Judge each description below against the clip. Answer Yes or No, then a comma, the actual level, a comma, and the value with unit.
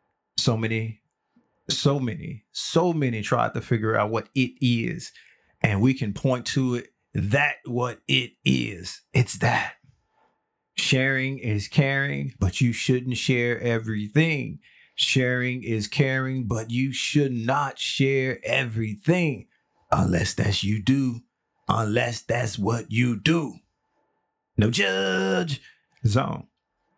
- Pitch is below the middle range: Yes, low, 120 Hz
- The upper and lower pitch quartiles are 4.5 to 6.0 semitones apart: No, average, 3.3 semitones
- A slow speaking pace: Yes, slow, 120 wpm